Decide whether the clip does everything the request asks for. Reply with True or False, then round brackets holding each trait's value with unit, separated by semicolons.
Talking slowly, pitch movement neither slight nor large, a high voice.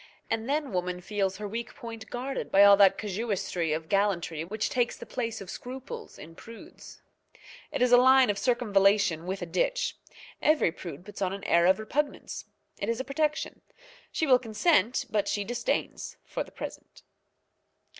False (175 wpm; 4.7 semitones; 210 Hz)